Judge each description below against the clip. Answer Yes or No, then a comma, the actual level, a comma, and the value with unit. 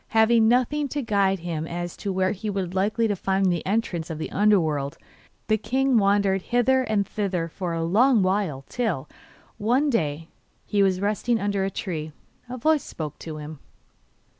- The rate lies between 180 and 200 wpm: Yes, average, 185 wpm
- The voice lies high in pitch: Yes, high, 195 Hz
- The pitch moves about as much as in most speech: Yes, average, 4.6 semitones